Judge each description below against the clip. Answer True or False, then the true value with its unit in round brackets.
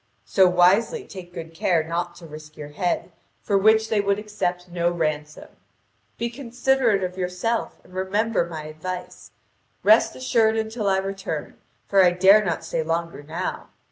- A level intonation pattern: False (4.0 semitones)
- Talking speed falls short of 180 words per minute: True (160 wpm)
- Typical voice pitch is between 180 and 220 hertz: True (185 Hz)